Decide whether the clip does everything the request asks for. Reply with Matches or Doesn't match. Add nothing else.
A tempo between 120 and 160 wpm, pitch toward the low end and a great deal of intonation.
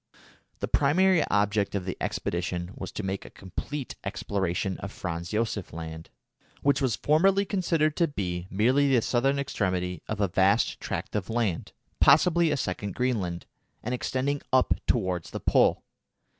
Matches